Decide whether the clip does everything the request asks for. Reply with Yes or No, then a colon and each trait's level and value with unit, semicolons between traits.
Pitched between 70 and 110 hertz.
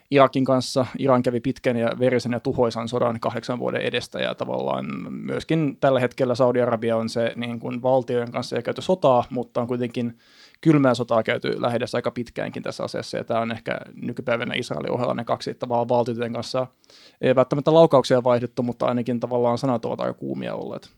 No: low, 125 Hz